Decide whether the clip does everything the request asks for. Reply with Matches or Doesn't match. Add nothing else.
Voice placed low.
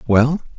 Matches